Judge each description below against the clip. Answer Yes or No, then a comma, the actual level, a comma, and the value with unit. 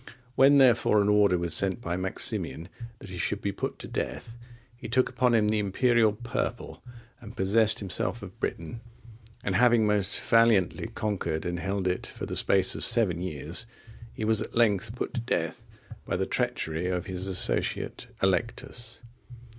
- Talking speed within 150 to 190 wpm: Yes, average, 170 wpm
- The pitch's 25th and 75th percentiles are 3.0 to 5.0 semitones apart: Yes, average, 3.9 semitones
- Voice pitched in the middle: No, low, 105 Hz